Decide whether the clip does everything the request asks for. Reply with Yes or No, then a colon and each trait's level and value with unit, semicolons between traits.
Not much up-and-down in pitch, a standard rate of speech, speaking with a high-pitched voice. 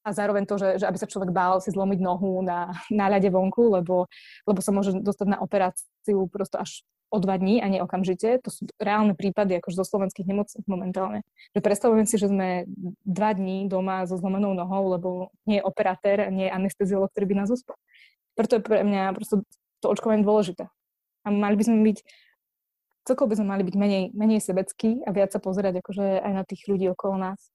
No: narrow, 1.7 semitones; fast, 205 wpm; high, 195 Hz